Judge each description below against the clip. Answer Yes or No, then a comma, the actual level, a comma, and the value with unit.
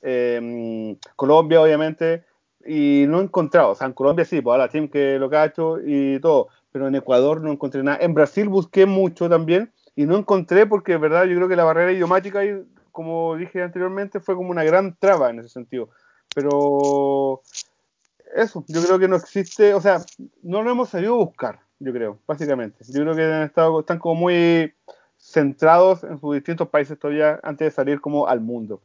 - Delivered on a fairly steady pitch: No, average, 4.6 semitones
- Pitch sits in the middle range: Yes, medium, 165 Hz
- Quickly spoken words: Yes, fast, 200 wpm